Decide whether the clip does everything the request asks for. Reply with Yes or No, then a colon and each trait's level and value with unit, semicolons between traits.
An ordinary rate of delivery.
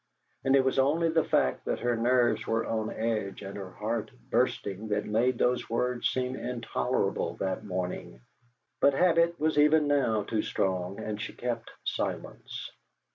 Yes: average, 160 wpm